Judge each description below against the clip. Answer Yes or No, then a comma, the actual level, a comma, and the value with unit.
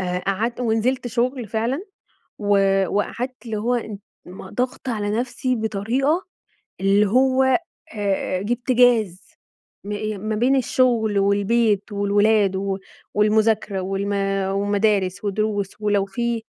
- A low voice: No, high, 215 Hz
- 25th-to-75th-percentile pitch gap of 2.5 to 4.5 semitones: Yes, average, 3.2 semitones